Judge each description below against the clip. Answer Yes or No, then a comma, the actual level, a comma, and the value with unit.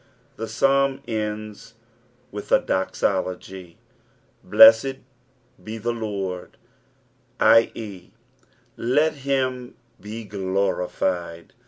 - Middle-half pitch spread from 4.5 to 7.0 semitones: Yes, average, 5.0 semitones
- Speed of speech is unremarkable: No, slow, 75 wpm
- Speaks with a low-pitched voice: Yes, low, 110 Hz